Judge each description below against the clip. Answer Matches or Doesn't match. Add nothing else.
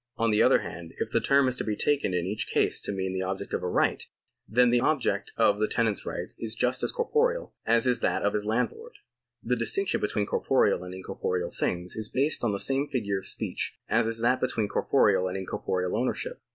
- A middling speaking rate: Doesn't match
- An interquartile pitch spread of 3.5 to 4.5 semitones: Doesn't match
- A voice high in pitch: Doesn't match